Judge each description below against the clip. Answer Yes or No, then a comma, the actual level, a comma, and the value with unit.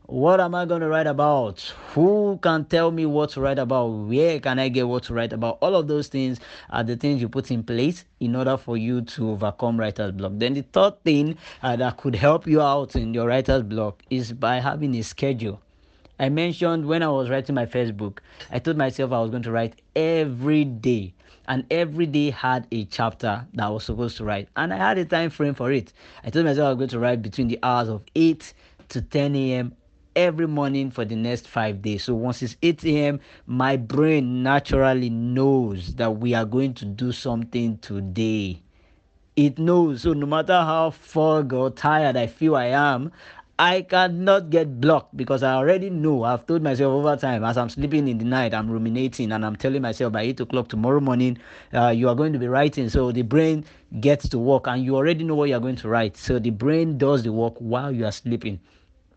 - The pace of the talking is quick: Yes, fast, 220 wpm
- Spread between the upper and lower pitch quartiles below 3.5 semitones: No, average, 4.2 semitones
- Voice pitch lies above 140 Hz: No, low, 130 Hz